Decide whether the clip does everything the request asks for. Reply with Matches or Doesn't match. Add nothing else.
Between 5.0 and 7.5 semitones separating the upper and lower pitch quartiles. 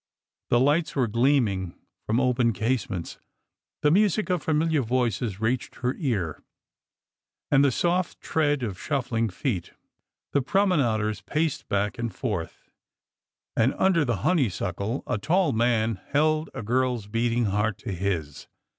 Matches